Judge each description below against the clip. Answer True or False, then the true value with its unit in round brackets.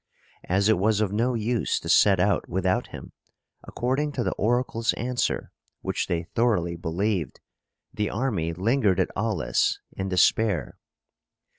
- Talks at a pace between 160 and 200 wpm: False (140 wpm)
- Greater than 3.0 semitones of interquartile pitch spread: True (4.2 semitones)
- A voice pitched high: False (105 Hz)